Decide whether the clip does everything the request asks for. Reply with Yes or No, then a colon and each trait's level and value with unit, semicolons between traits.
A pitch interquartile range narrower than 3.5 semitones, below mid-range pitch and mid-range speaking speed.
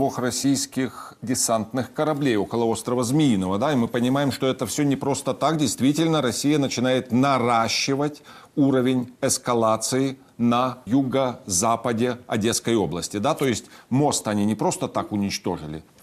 Yes: average, 3.0 semitones; low, 125 Hz; average, 135 wpm